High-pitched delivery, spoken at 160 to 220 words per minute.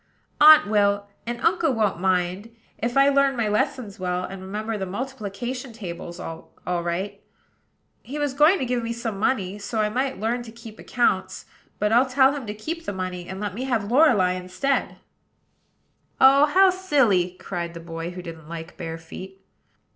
Yes: high, 210 Hz; average, 175 wpm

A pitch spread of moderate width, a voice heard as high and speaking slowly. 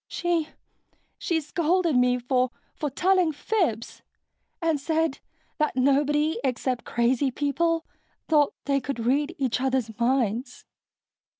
Yes: average, 4.2 semitones; very high, 280 Hz; slow, 115 wpm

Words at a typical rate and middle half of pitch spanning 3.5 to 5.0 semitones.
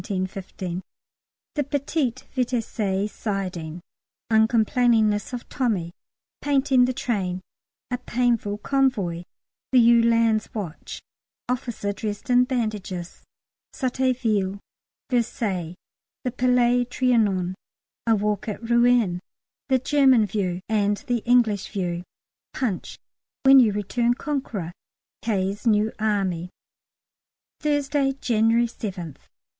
No: slow, 95 wpm; average, 4.1 semitones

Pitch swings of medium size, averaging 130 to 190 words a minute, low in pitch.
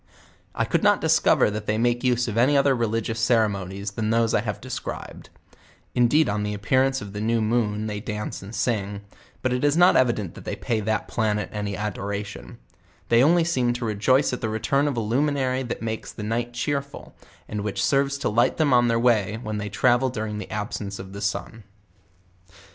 No: average, 3.2 semitones; fast, 205 wpm; low, 115 Hz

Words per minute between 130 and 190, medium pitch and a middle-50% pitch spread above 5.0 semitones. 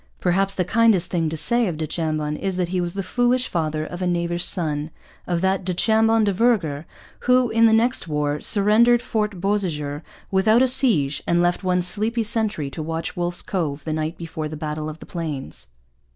No: average, 200 wpm; medium, 180 Hz; wide, 5.5 semitones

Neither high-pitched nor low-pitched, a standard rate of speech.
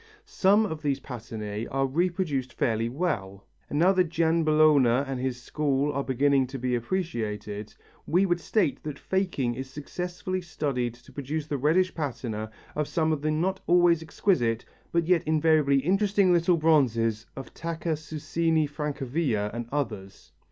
Yes: medium, 150 Hz; average, 150 wpm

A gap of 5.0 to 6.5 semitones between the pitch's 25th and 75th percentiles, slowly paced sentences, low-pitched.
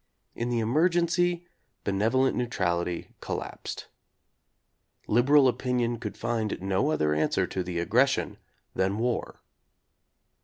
Yes: wide, 5.5 semitones; slow, 110 wpm; low, 120 Hz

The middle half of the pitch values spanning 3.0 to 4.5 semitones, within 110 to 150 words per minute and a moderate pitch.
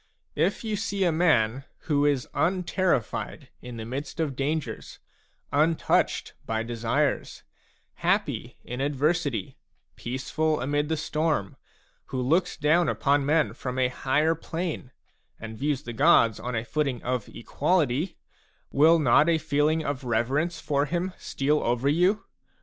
Yes: average, 4.2 semitones; average, 140 wpm; medium, 145 Hz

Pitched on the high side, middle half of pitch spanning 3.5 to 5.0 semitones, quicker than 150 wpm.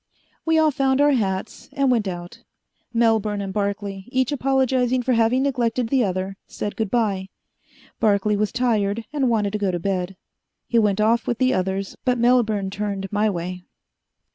Yes: high, 215 Hz; average, 4.1 semitones; average, 170 wpm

